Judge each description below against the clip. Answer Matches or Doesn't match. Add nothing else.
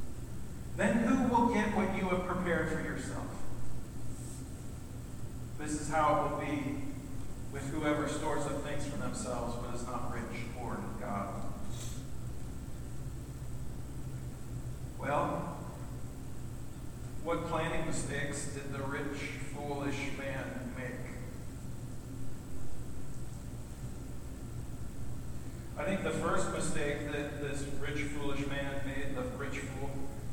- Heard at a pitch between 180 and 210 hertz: Doesn't match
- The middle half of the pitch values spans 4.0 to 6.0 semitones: Doesn't match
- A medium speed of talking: Doesn't match